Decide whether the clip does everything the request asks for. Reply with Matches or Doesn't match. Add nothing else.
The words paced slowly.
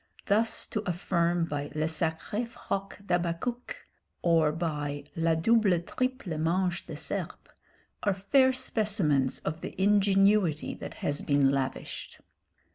Matches